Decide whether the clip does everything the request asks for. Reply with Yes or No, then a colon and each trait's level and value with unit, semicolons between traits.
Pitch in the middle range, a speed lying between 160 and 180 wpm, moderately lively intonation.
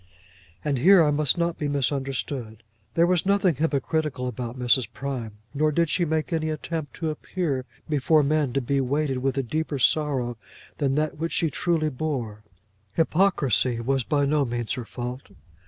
Yes: medium, 145 Hz; average, 170 wpm; average, 3.6 semitones